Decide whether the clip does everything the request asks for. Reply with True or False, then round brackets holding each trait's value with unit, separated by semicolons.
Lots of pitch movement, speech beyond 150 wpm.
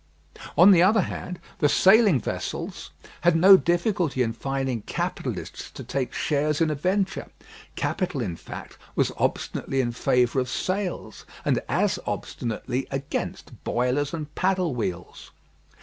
False (6.4 semitones; 135 wpm)